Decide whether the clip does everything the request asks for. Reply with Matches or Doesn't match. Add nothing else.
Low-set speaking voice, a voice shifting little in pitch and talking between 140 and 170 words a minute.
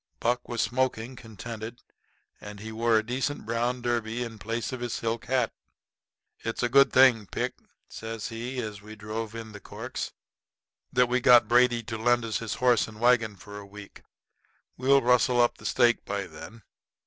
Doesn't match